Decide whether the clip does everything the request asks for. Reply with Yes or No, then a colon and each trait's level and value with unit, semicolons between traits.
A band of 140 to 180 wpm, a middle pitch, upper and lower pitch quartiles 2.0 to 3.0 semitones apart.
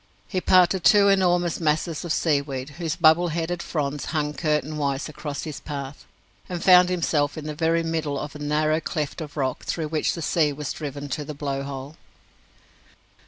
Yes: average, 175 wpm; medium, 155 Hz; narrow, 2.5 semitones